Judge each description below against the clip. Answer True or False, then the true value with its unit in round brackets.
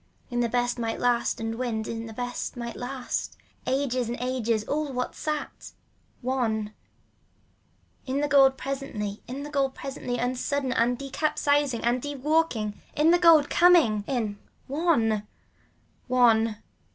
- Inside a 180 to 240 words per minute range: False (135 wpm)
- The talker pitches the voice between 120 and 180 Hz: False (250 Hz)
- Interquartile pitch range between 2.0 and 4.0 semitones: True (3.6 semitones)